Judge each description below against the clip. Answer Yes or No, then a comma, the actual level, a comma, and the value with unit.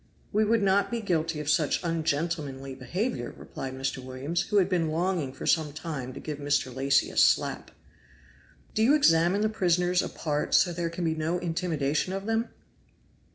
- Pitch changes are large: No, average, 4.3 semitones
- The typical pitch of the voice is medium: Yes, medium, 165 Hz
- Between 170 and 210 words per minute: Yes, average, 180 wpm